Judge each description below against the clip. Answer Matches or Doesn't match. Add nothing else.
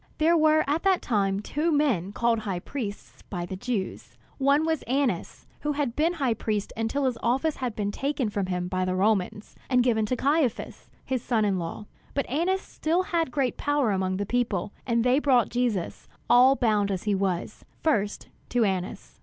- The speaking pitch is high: Matches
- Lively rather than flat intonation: Matches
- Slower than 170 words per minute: Doesn't match